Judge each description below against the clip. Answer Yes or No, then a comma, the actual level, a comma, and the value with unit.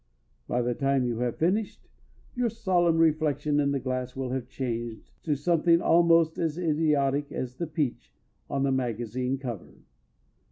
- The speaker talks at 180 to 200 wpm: No, average, 160 wpm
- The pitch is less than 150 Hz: Yes, medium, 140 Hz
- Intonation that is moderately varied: Yes, average, 4.5 semitones